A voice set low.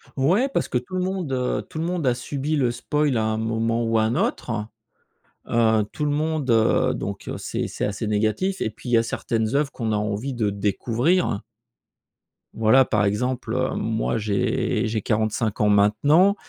Yes: low, 115 Hz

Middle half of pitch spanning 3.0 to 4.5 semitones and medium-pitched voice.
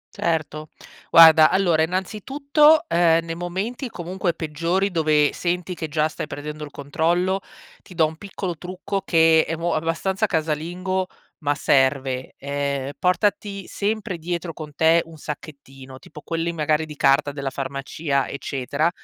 Yes: average, 3.4 semitones; medium, 165 Hz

